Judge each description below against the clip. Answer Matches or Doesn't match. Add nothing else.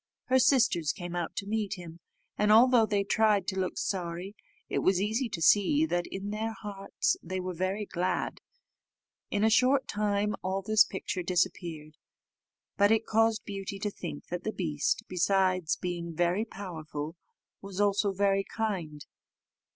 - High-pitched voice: Matches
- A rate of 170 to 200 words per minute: Doesn't match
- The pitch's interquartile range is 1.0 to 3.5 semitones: Matches